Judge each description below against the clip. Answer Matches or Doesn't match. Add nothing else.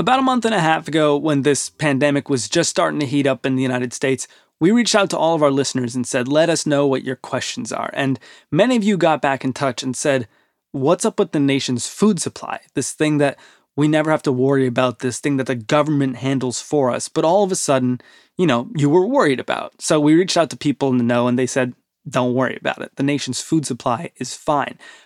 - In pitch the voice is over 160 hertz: Doesn't match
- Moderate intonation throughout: Matches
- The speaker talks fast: Matches